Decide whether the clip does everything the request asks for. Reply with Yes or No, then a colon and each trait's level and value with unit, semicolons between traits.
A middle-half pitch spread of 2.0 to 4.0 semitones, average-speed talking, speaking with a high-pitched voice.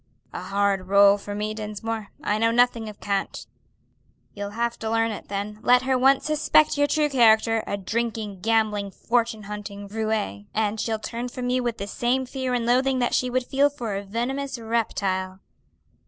Yes: average, 3.3 semitones; average, 185 wpm; high, 225 Hz